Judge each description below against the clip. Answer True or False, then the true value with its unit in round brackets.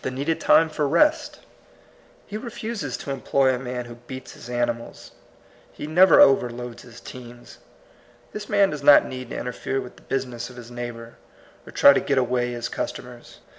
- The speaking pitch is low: True (125 Hz)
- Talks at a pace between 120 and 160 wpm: False (175 wpm)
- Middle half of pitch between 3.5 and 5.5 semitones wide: False (3.1 semitones)